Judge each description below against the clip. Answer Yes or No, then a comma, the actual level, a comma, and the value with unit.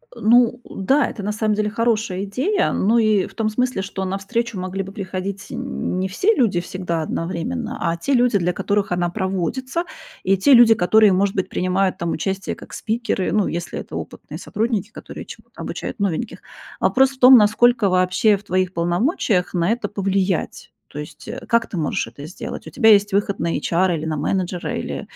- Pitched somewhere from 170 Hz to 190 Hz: No, high, 200 Hz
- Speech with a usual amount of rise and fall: Yes, average, 3.8 semitones